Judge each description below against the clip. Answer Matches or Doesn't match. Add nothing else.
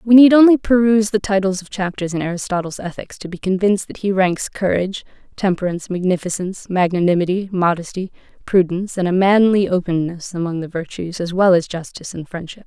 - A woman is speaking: Matches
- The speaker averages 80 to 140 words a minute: Doesn't match